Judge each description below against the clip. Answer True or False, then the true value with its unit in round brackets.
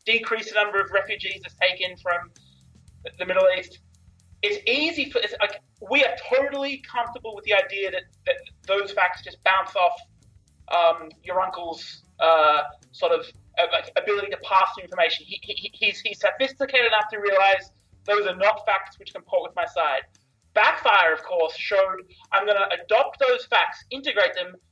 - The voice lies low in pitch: False (195 Hz)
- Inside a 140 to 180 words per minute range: True (175 wpm)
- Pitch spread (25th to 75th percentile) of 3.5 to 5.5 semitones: True (4.5 semitones)